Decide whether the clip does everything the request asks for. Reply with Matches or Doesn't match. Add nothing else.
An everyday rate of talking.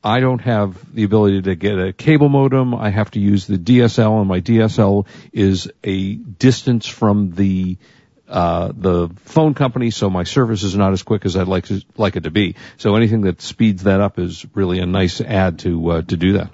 Doesn't match